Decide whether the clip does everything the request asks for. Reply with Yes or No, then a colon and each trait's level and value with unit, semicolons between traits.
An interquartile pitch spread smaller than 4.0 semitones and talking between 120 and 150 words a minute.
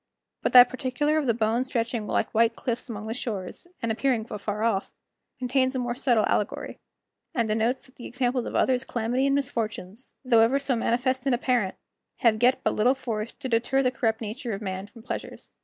No: narrow, 2.6 semitones; average, 200 wpm